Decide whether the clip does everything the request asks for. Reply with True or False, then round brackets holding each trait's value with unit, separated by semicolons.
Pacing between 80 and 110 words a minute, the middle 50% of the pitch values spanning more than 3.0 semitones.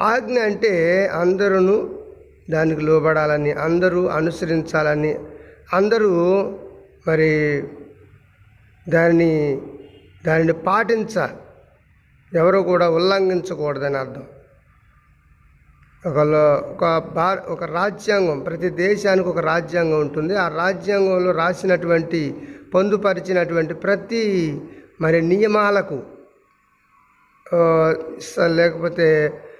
False (70 wpm; 3.7 semitones)